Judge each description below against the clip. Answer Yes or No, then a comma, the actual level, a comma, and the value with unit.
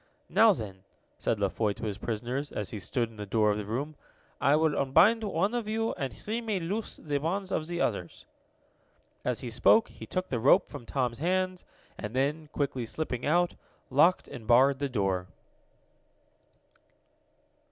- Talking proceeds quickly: No, average, 175 wpm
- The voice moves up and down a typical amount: No, wide, 7.7 semitones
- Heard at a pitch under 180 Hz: Yes, medium, 140 Hz